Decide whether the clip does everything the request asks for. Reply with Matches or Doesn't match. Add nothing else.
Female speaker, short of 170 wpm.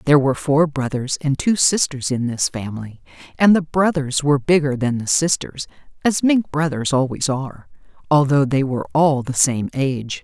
Doesn't match